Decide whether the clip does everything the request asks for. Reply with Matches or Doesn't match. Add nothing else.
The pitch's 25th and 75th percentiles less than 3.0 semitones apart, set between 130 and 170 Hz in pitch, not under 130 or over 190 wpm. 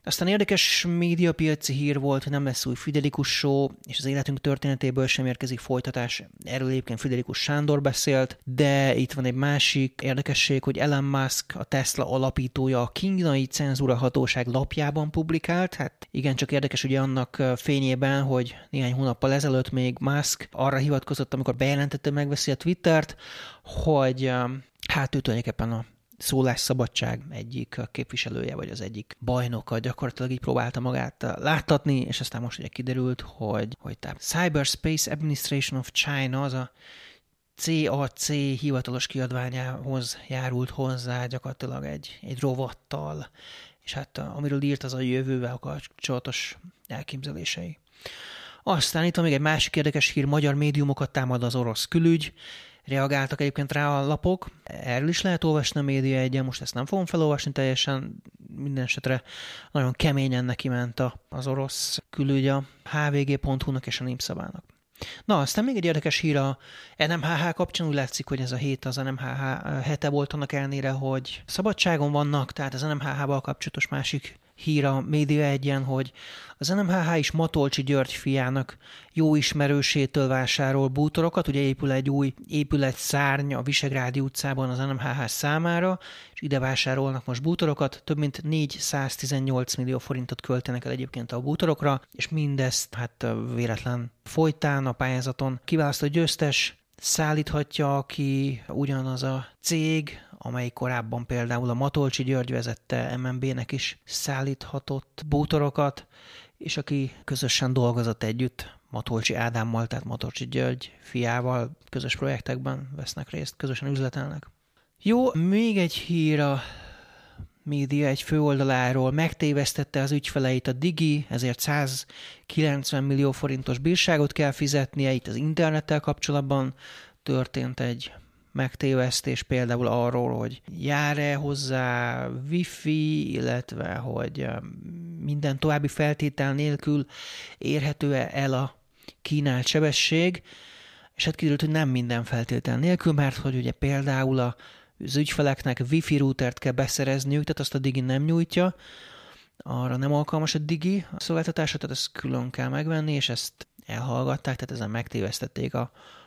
Matches